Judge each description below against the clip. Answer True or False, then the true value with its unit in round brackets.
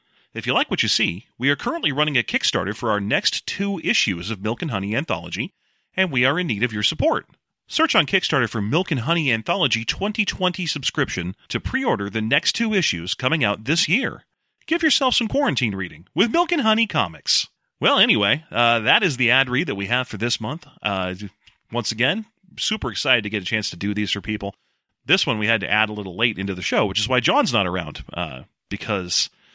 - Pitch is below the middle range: True (125 Hz)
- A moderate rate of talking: False (220 wpm)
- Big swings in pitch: True (8.8 semitones)